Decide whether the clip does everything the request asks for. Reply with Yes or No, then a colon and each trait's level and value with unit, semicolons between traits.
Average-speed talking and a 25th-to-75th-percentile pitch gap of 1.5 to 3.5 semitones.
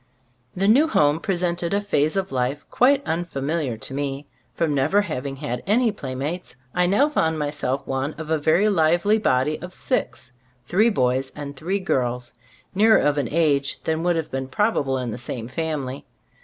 No: average, 180 wpm; wide, 5.4 semitones